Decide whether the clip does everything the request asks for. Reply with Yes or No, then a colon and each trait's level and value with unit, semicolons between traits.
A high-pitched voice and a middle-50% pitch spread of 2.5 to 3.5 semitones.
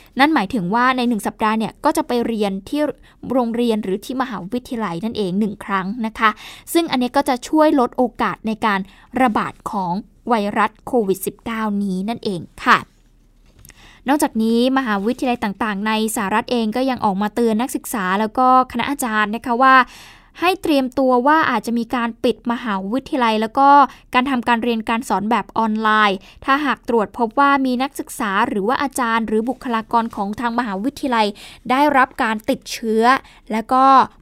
Yes: high, 235 Hz; average, 3.1 semitones